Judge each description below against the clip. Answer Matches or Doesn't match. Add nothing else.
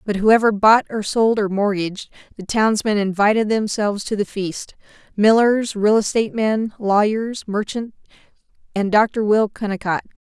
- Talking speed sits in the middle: Doesn't match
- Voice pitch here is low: Doesn't match